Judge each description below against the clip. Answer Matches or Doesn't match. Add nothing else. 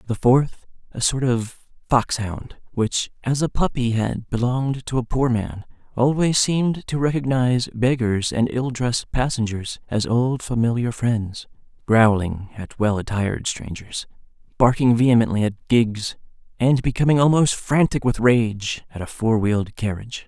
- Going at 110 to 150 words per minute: Matches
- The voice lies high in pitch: Doesn't match